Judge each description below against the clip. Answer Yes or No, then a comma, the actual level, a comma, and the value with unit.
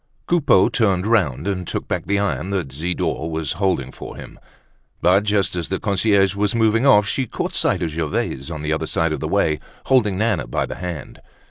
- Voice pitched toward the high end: No, very low, 95 Hz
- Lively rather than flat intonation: No, average, 4.4 semitones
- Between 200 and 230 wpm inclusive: Yes, fast, 205 wpm